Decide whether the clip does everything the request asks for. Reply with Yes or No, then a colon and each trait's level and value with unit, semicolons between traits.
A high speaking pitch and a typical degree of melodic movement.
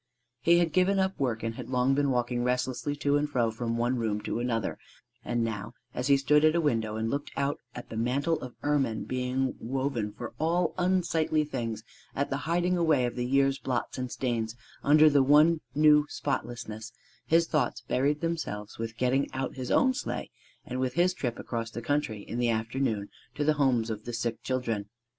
No: low, 130 Hz; average, 4.1 semitones